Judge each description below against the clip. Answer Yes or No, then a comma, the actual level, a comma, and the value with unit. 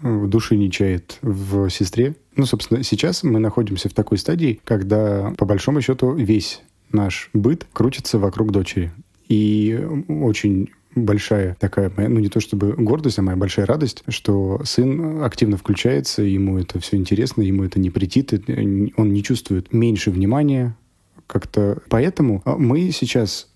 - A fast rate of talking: No, average, 150 wpm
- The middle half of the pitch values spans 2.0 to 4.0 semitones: Yes, average, 3.7 semitones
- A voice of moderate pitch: No, low, 105 Hz